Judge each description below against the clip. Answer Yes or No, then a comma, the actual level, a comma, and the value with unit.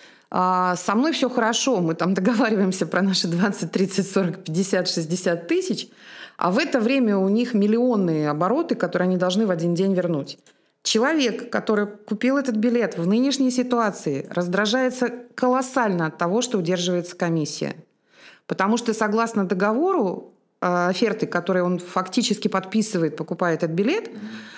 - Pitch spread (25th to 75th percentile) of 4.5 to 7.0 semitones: Yes, average, 4.9 semitones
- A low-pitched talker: No, high, 200 Hz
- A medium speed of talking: Yes, average, 140 wpm